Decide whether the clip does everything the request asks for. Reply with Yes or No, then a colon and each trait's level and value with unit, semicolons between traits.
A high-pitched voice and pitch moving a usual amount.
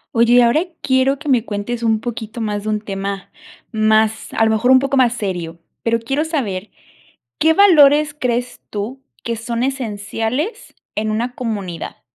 Yes: high, 230 Hz; average, 3.5 semitones